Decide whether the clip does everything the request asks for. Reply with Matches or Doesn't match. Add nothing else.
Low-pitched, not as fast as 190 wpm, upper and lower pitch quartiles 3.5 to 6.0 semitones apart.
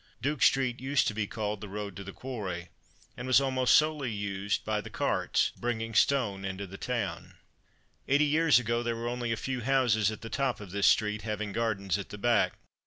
Doesn't match